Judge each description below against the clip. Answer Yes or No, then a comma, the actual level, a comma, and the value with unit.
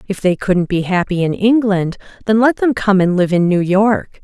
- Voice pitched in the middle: No, high, 195 Hz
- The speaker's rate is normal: No, fast, 225 wpm